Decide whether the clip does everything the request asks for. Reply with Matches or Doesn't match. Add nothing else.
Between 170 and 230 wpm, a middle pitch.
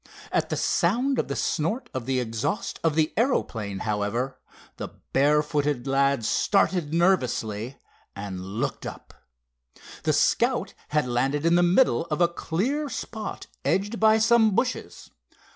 Doesn't match